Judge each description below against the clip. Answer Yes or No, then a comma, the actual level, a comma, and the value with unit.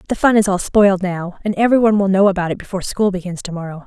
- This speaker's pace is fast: Yes, fast, 265 wpm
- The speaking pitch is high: Yes, high, 195 Hz